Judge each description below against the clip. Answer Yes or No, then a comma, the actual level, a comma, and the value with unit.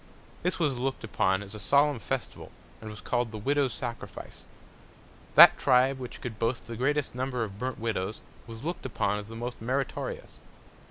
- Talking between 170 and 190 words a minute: Yes, average, 180 wpm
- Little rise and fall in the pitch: No, average, 3.3 semitones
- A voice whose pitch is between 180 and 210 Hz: No, low, 120 Hz